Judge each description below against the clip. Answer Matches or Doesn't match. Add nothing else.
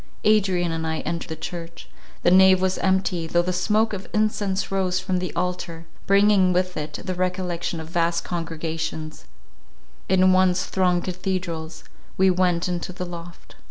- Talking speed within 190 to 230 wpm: Doesn't match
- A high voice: Doesn't match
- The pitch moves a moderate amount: Doesn't match